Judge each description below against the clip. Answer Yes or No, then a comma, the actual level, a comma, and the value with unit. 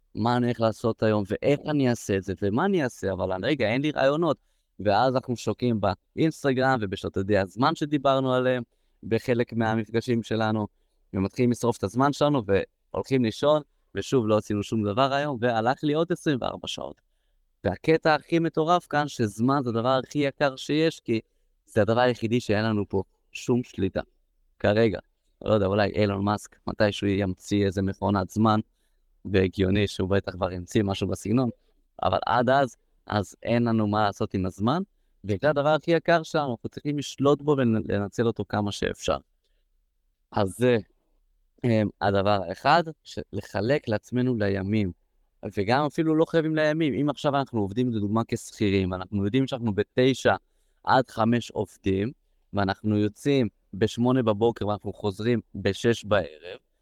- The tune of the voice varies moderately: Yes, average, 4.7 semitones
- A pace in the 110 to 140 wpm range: No, fast, 150 wpm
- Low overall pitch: Yes, low, 115 Hz